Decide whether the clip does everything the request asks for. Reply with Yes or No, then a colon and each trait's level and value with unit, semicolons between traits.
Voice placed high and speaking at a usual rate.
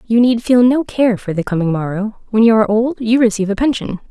No: high, 220 Hz; fast, 250 wpm